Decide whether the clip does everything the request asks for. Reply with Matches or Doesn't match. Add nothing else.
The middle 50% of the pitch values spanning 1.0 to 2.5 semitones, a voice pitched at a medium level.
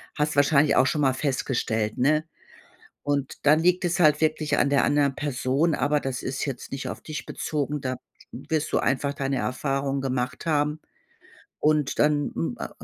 Matches